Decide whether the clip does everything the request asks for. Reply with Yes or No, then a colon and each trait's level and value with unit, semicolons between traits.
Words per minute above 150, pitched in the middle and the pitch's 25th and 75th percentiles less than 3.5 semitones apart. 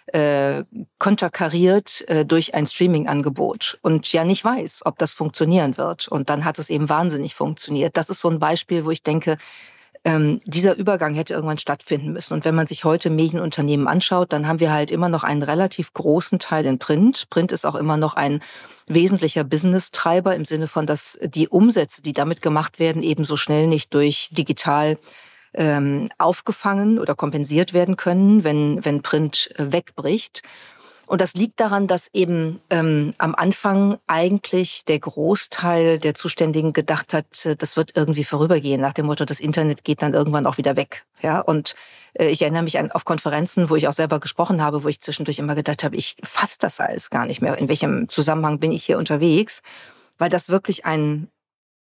Yes: average, 180 wpm; medium, 160 Hz; average, 2.8 semitones